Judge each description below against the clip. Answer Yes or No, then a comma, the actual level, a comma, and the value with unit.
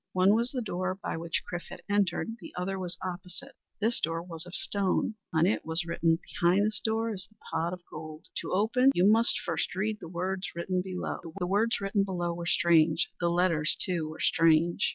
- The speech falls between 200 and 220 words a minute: Yes, fast, 205 wpm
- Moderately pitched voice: Yes, medium, 180 Hz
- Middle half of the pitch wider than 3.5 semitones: No, average, 3.0 semitones